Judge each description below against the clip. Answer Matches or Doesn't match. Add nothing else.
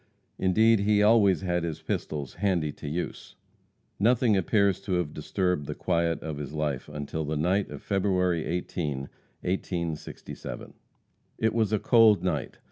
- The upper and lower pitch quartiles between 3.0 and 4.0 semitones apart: Doesn't match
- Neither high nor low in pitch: Doesn't match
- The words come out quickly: Doesn't match